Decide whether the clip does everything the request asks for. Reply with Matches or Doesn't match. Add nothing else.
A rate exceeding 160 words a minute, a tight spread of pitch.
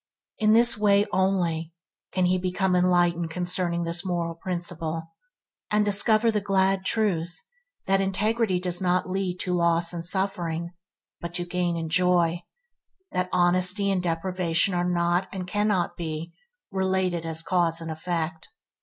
Doesn't match